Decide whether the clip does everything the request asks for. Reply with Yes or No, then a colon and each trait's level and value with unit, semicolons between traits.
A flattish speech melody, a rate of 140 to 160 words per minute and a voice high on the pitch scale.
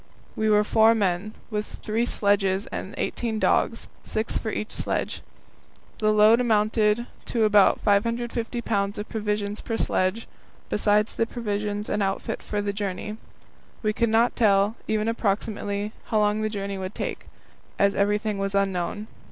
Yes: narrow, 1.5 semitones; average, 150 wpm; high, 210 Hz